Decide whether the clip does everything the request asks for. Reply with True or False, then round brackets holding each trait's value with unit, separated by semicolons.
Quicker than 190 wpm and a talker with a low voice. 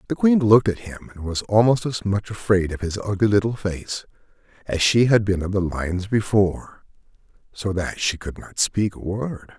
True (200 wpm; 100 Hz)